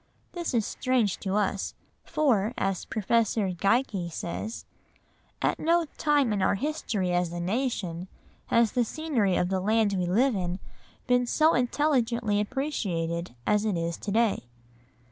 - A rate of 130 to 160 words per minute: Yes, average, 145 wpm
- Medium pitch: No, high, 215 Hz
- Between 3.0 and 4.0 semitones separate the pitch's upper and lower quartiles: No, average, 5.1 semitones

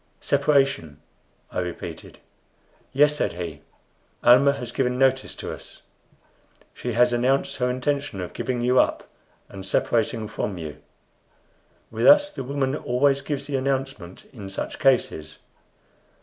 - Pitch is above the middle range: No, low, 125 Hz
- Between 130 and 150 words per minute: Yes, slow, 135 wpm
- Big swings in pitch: No, average, 4.8 semitones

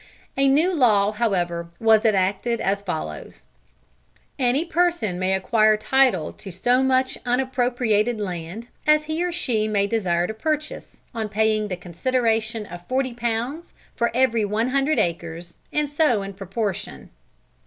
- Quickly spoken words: No, average, 145 wpm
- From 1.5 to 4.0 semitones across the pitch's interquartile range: No, average, 4.8 semitones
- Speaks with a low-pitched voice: No, high, 225 Hz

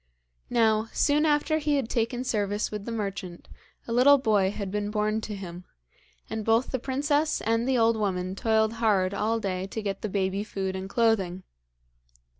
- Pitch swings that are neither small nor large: Yes, average, 3.1 semitones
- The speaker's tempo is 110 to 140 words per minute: No, average, 180 wpm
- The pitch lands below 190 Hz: No, high, 215 Hz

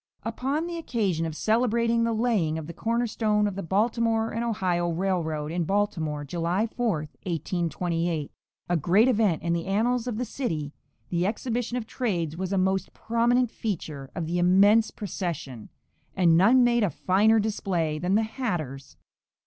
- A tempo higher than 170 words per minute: No, average, 160 wpm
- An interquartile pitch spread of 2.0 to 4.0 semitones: No, average, 5.2 semitones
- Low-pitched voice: No, high, 195 Hz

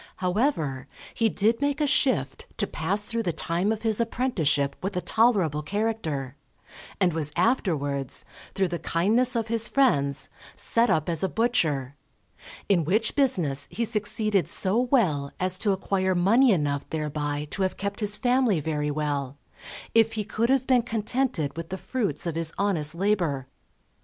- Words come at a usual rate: Yes, average, 160 wpm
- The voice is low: No, high, 190 Hz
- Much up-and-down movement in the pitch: Yes, wide, 7.0 semitones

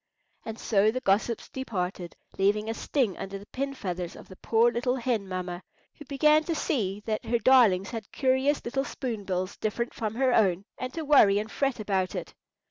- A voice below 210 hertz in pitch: No, high, 225 Hz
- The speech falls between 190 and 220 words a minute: Yes, average, 195 wpm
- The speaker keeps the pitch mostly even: No, average, 4.8 semitones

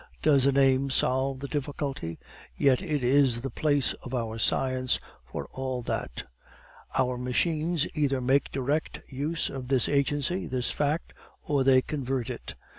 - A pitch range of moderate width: No, narrow, 2.1 semitones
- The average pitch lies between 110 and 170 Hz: Yes, low, 135 Hz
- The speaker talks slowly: No, average, 150 wpm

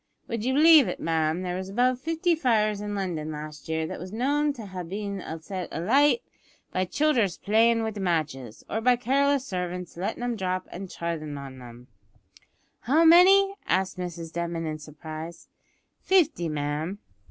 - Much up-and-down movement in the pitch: Yes, wide, 7.1 semitones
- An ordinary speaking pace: Yes, average, 165 wpm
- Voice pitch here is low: No, high, 190 Hz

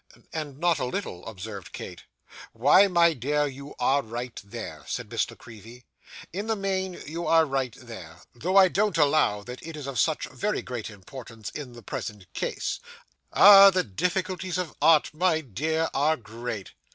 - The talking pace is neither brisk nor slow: Yes, average, 175 wpm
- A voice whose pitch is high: No, medium, 145 Hz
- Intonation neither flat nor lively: No, wide, 6.6 semitones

